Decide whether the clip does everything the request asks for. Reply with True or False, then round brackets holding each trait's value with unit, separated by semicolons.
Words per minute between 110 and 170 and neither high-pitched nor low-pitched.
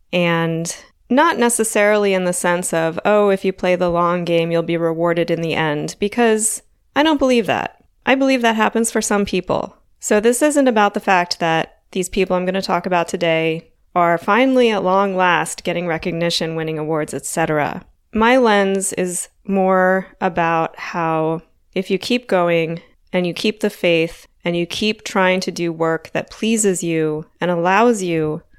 False (180 wpm; 180 Hz)